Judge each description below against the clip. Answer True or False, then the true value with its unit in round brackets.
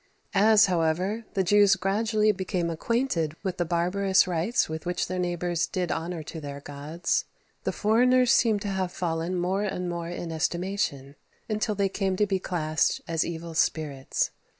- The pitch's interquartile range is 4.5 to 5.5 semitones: False (3.4 semitones)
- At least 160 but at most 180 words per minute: True (170 wpm)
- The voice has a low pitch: False (180 Hz)